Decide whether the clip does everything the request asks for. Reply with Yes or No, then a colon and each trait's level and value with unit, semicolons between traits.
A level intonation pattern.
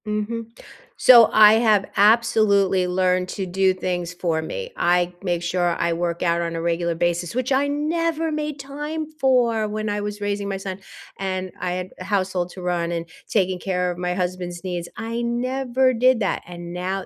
No: average, 4.6 semitones